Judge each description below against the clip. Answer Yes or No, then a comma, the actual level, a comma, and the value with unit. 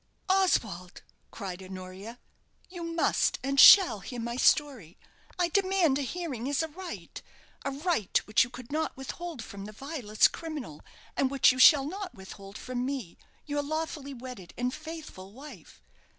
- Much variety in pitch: Yes, wide, 6.7 semitones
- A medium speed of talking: Yes, average, 155 wpm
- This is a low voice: No, very high, 265 Hz